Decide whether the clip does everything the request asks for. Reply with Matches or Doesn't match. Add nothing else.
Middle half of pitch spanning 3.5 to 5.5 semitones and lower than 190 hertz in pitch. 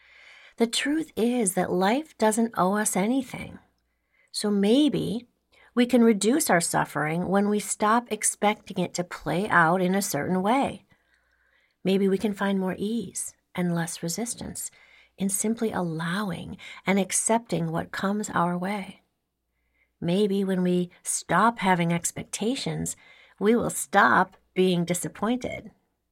Doesn't match